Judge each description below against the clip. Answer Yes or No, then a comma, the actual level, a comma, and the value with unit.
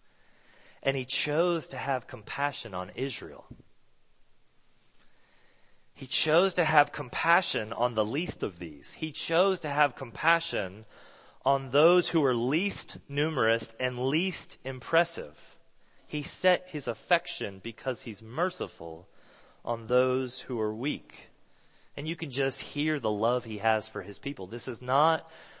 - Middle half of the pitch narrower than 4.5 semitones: No, average, 5.2 semitones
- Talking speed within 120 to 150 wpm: Yes, average, 140 wpm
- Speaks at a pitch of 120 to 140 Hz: Yes, low, 135 Hz